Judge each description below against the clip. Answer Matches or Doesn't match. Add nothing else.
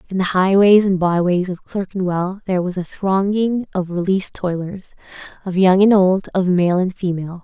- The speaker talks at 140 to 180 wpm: Matches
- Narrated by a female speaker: Matches